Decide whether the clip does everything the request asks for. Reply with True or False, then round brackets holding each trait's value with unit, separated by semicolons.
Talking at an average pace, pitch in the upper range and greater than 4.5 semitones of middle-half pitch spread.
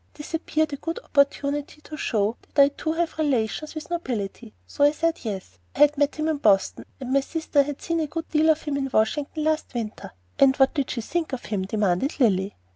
False (225 wpm; 285 Hz; 5.3 semitones)